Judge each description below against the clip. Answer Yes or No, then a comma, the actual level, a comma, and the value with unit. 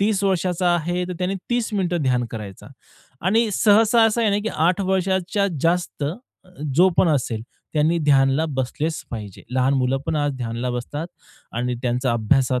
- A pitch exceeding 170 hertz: No, medium, 160 Hz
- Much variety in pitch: Yes, wide, 6.9 semitones